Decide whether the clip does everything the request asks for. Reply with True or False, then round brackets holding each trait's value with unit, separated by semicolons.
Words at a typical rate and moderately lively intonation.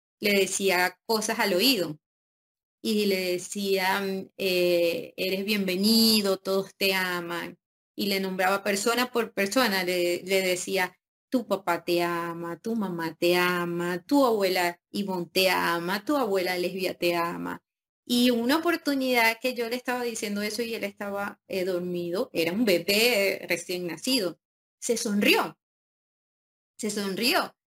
True (140 wpm; 3.9 semitones)